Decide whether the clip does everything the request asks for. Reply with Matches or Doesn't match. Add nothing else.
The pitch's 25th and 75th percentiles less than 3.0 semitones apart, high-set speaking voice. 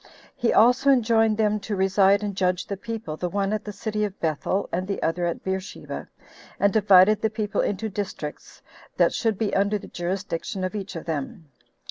Matches